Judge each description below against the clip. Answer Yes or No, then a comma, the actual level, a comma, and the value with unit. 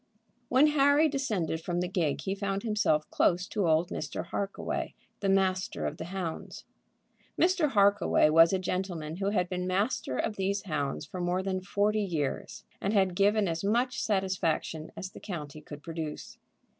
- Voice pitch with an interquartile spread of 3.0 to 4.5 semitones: Yes, average, 3.6 semitones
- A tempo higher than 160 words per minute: Yes, average, 170 wpm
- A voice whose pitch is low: No, high, 190 Hz